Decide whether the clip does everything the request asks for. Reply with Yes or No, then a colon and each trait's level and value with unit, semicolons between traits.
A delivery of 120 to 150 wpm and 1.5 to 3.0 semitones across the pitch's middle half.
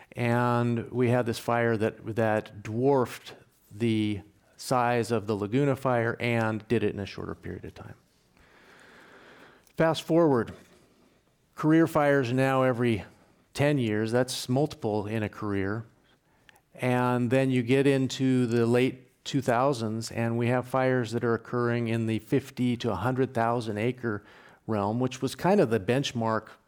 Yes: average, 145 wpm; average, 2.7 semitones